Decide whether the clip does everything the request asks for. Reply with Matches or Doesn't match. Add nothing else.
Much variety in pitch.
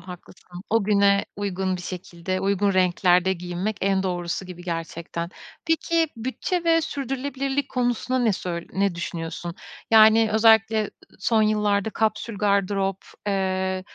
Doesn't match